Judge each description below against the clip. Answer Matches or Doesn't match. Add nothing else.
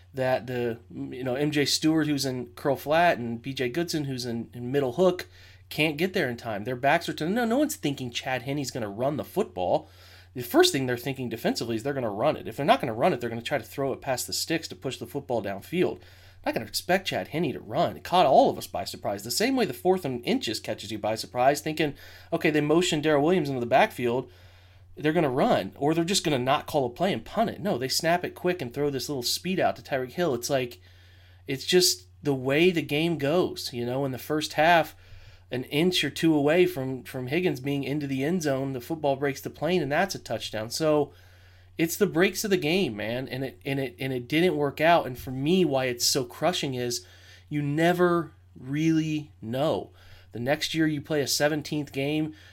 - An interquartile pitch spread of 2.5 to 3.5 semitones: Doesn't match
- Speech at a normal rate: Doesn't match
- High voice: Doesn't match